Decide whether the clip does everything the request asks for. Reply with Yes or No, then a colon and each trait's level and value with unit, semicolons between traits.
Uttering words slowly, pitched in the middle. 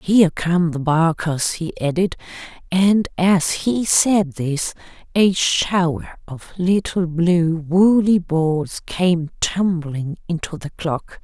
Yes: slow, 125 wpm; medium, 170 Hz